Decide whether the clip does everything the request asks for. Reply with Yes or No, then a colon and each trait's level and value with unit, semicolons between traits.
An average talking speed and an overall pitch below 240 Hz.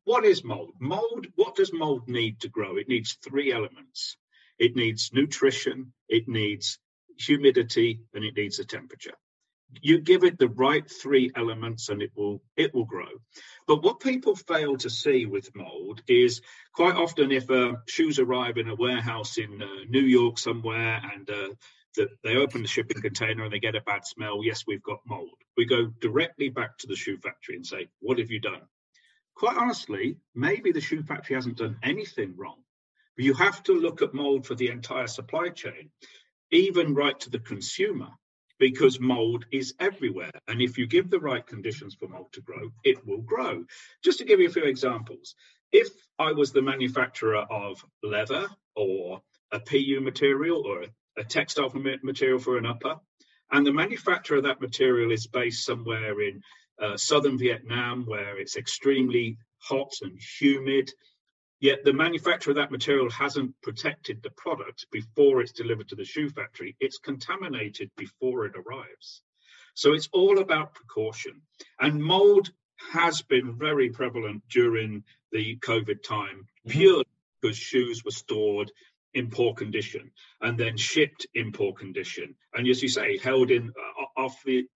Yes: average, 170 wpm; low, 135 Hz